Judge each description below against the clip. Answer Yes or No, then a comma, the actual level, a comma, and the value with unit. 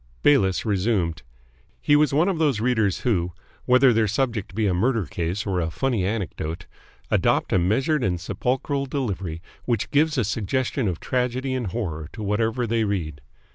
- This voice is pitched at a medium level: No, low, 110 Hz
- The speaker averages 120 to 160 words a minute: No, average, 170 wpm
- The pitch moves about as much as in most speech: No, wide, 5.7 semitones